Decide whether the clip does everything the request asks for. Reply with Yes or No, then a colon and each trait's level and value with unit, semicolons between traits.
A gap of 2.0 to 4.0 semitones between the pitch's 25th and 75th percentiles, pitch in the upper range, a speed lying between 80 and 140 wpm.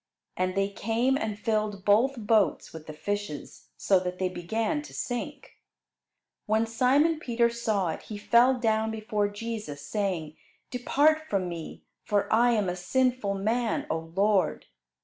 No: average, 3.7 semitones; high, 215 Hz; average, 150 wpm